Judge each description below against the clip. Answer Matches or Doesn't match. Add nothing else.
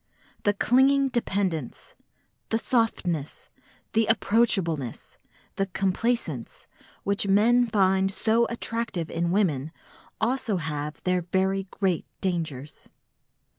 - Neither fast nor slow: Doesn't match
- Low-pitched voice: Doesn't match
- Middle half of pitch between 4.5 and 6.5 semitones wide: Matches